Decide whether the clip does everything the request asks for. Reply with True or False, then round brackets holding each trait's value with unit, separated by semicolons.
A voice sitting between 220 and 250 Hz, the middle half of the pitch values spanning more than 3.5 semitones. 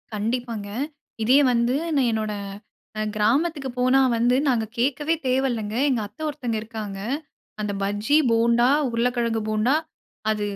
False (235 Hz; 2.9 semitones)